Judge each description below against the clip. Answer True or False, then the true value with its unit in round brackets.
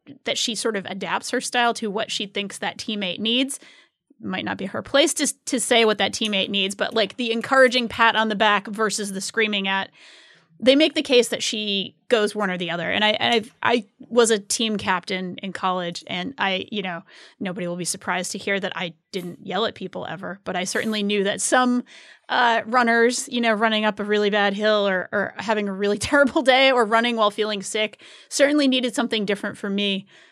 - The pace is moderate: False (220 wpm)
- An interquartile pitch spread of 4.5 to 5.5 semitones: False (3.3 semitones)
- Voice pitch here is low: False (215 Hz)